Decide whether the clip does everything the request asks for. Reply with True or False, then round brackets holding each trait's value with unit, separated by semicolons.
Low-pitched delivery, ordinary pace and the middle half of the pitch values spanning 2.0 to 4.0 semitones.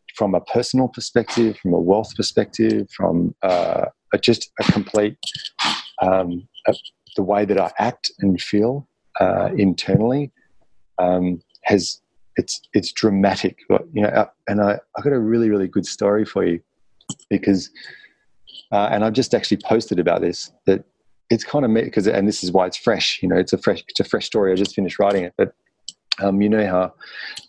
True (100 Hz; 185 wpm; 2.9 semitones)